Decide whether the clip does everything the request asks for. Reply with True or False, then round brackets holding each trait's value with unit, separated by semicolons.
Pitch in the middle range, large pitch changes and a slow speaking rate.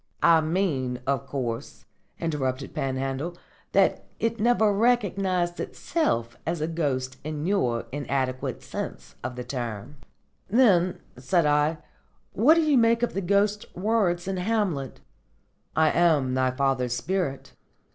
True (160 Hz; 7.0 semitones; 130 wpm)